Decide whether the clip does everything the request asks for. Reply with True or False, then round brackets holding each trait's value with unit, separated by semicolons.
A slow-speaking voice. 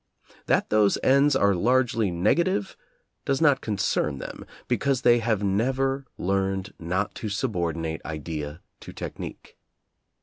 True (125 wpm)